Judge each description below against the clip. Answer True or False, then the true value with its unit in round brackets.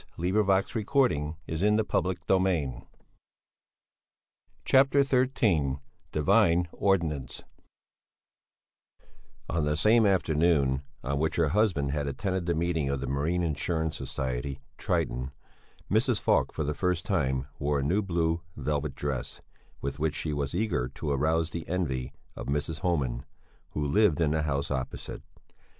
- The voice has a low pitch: True (80 Hz)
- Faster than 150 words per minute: False (135 wpm)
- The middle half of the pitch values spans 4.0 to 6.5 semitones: True (4.4 semitones)